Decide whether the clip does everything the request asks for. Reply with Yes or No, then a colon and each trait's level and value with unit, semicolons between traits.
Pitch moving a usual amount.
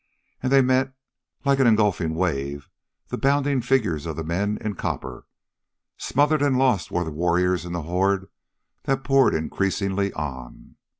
No: wide, 7.6 semitones